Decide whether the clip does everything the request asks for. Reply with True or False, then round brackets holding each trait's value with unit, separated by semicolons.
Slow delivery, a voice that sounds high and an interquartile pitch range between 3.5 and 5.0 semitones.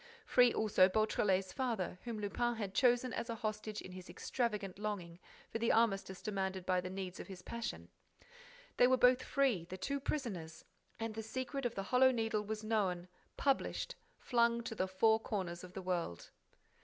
False (180 wpm; 215 Hz; 4.0 semitones)